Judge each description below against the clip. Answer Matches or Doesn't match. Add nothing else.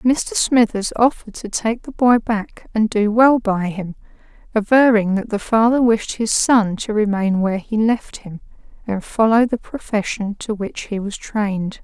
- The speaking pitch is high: Matches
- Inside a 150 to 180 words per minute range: Matches